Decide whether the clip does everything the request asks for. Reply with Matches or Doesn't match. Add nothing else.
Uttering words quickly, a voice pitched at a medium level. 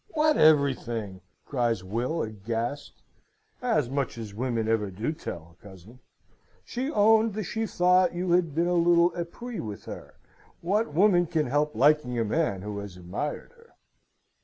Doesn't match